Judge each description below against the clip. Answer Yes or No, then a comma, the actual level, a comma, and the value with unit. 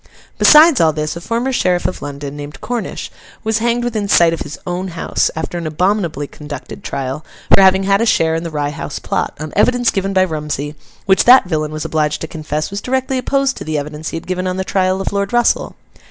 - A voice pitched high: No, medium, 180 Hz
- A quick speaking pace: Yes, fast, 225 wpm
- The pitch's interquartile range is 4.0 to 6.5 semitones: Yes, average, 5.2 semitones